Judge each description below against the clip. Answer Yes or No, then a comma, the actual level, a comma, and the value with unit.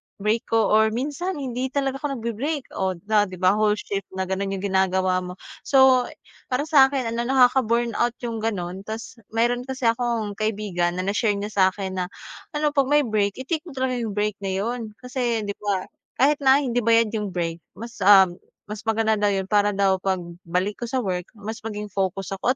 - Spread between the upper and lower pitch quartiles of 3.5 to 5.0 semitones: Yes, average, 4.1 semitones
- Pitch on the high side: Yes, high, 220 Hz